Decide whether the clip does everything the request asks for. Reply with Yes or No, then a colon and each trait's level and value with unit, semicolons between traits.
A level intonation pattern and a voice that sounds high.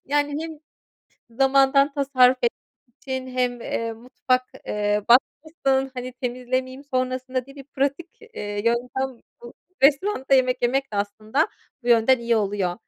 Yes: narrow, 2.3 semitones; very high, 255 Hz